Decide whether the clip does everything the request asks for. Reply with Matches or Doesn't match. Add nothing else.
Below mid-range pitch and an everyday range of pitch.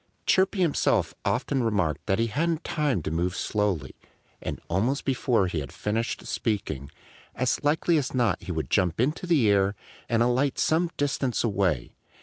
Doesn't match